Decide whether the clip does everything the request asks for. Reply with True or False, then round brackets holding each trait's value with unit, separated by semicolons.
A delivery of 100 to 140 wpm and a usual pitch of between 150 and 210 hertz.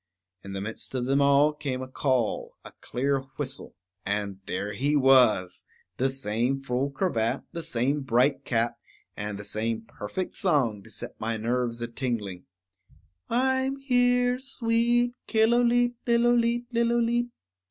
False (135 wpm; 135 Hz)